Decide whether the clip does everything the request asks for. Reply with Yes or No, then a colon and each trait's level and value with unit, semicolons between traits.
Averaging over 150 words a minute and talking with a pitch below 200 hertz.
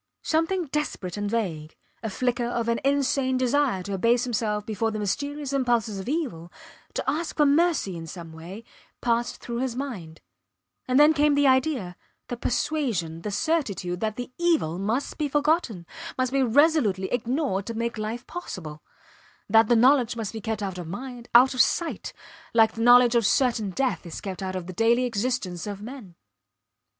No: average, 180 wpm; high, 235 Hz